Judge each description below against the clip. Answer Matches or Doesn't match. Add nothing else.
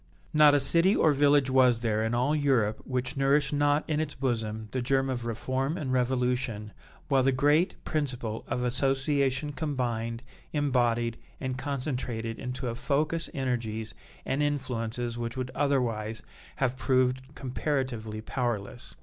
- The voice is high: Doesn't match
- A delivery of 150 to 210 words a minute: Doesn't match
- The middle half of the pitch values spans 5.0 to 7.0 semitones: Doesn't match